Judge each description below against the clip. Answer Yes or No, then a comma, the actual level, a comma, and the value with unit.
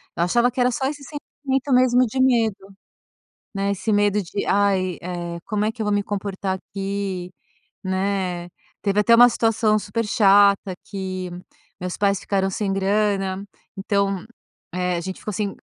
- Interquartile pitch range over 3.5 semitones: No, narrow, 2.4 semitones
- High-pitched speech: Yes, high, 200 Hz